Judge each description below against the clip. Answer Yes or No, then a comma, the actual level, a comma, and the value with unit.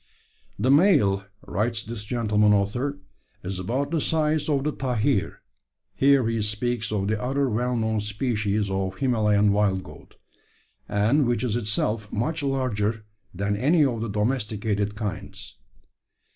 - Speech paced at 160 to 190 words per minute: No, average, 140 wpm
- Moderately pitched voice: No, low, 110 Hz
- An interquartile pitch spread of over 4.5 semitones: No, average, 3.9 semitones